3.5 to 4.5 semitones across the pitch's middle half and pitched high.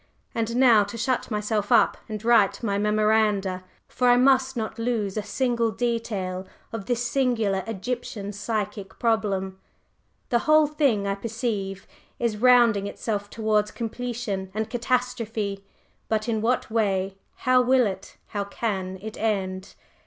No: average, 3.1 semitones; high, 220 Hz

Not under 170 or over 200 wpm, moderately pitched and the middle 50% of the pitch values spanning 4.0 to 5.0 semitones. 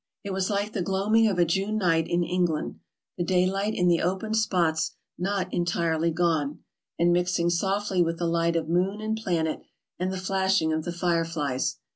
No: average, 185 wpm; medium, 175 Hz; narrow, 2.5 semitones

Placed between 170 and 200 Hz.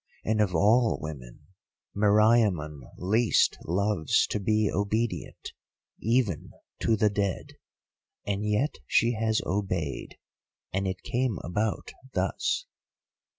No: low, 105 Hz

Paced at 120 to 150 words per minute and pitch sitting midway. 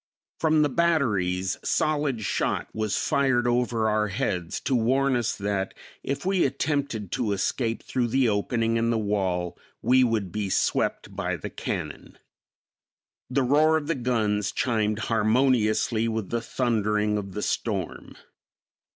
No: average, 140 wpm; low, 115 Hz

